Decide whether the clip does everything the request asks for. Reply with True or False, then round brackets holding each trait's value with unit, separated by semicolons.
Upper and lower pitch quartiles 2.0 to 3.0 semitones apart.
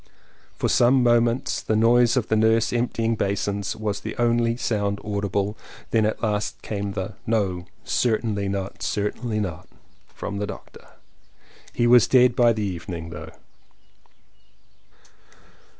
True (2.7 semitones)